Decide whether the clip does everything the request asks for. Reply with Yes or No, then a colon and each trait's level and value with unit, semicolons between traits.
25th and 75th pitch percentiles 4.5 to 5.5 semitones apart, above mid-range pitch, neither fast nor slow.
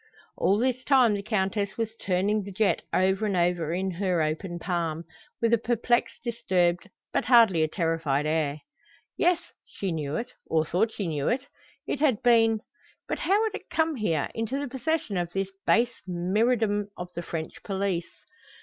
Yes: average, 5.2 semitones; high, 200 Hz; average, 175 wpm